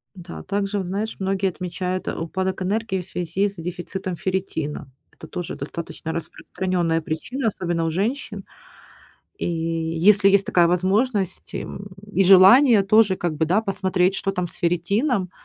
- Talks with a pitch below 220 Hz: Yes, medium, 185 Hz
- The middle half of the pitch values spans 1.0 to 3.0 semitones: Yes, narrow, 2.5 semitones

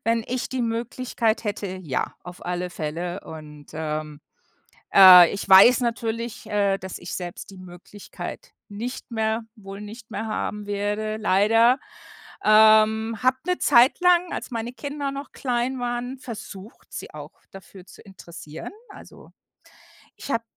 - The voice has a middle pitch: No, high, 215 Hz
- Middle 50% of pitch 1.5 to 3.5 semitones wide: No, average, 4.1 semitones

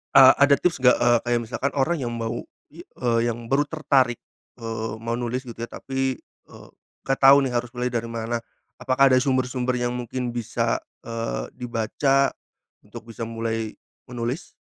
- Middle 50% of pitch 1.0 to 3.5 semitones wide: Yes, narrow, 2.4 semitones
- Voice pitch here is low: Yes, low, 120 Hz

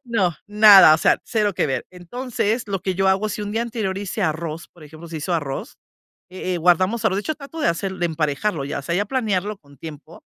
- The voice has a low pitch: No, high, 190 Hz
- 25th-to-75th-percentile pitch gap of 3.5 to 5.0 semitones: Yes, average, 4.5 semitones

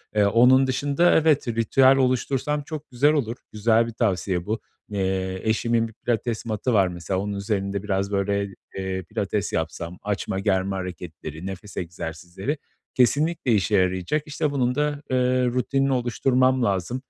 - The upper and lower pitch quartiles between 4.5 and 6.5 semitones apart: Yes, average, 5.1 semitones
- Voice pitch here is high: No, low, 110 Hz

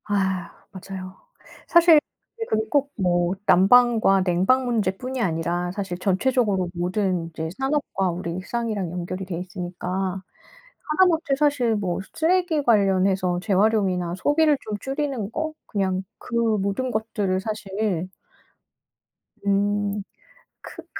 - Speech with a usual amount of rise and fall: Yes, average, 4.8 semitones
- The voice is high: Yes, high, 200 Hz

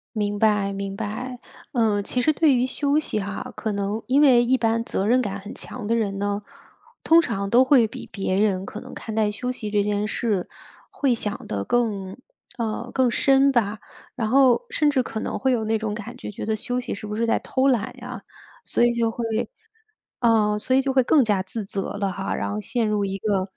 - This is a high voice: Yes, high, 220 Hz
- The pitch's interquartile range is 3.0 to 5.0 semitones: Yes, average, 3.5 semitones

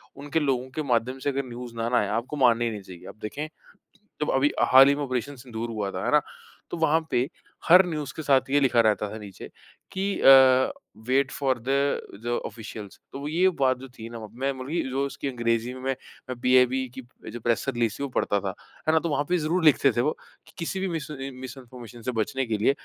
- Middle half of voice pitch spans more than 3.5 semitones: No, average, 3.2 semitones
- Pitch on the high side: No, low, 130 Hz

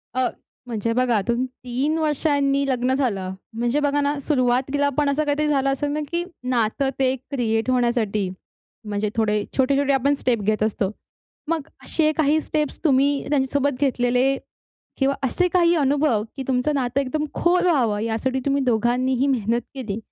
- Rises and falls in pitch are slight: No, average, 3.2 semitones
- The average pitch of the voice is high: Yes, very high, 265 Hz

